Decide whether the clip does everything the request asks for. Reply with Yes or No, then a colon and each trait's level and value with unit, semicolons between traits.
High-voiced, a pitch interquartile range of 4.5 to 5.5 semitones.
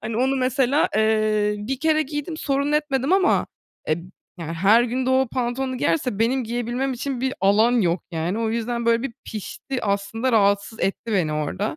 No: high, 235 Hz; average, 4.1 semitones